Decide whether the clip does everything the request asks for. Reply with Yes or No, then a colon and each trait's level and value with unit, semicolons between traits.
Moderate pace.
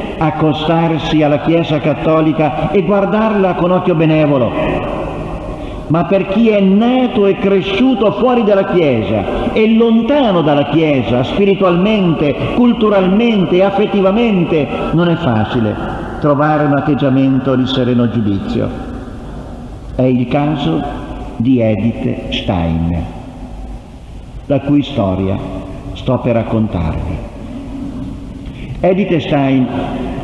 No: slow, 95 wpm